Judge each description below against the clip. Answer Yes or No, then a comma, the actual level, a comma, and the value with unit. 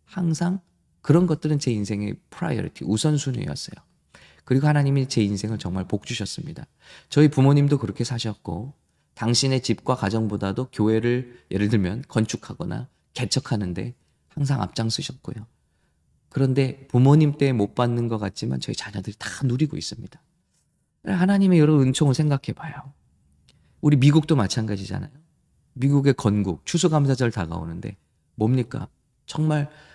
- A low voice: Yes, low, 125 Hz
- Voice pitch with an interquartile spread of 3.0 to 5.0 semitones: No, wide, 5.5 semitones